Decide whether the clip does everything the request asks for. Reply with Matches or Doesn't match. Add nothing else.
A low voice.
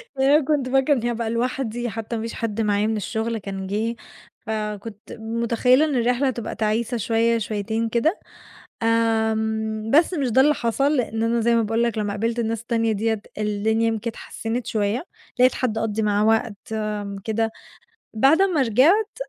Doesn't match